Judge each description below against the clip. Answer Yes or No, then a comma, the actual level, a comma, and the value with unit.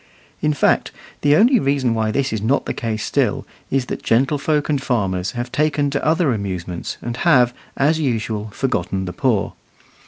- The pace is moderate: Yes, average, 175 wpm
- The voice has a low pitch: Yes, low, 125 Hz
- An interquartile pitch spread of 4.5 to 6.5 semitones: Yes, average, 4.9 semitones